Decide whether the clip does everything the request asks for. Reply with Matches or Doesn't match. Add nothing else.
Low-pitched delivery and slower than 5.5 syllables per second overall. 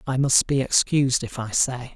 Matches